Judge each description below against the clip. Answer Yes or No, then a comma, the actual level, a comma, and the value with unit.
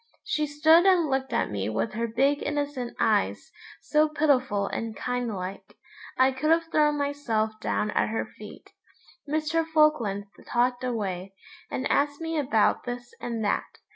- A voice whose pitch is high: Yes, very high, 260 Hz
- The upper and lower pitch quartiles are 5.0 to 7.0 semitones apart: Yes, wide, 5.4 semitones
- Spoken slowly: No, average, 155 wpm